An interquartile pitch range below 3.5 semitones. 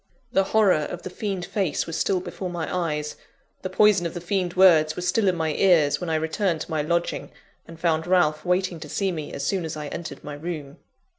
Yes: average, 2.9 semitones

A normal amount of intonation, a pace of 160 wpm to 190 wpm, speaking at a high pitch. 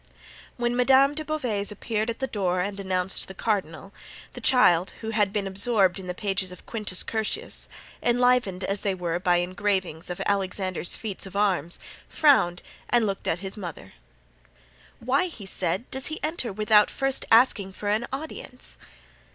Yes: average, 4.4 semitones; average, 165 wpm; high, 205 Hz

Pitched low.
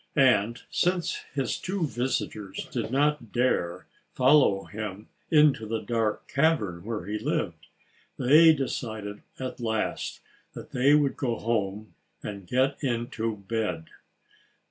Yes: low, 120 Hz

